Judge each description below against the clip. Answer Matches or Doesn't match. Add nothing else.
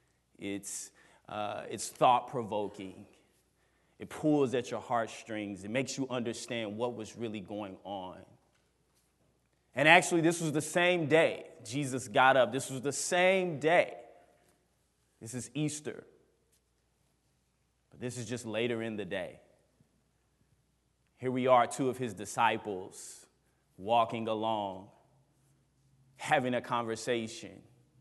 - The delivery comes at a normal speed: Doesn't match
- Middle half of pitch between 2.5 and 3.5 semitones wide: Doesn't match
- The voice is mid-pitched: Doesn't match